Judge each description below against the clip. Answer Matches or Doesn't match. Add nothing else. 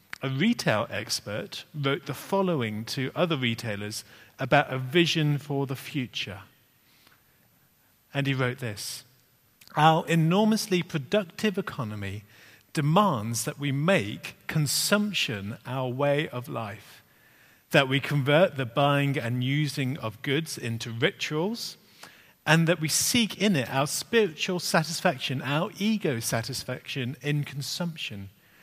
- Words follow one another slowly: Matches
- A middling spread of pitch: Matches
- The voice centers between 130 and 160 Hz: Matches